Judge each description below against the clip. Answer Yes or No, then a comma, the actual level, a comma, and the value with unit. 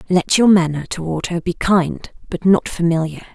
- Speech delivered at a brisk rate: No, average, 180 wpm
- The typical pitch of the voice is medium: Yes, medium, 175 Hz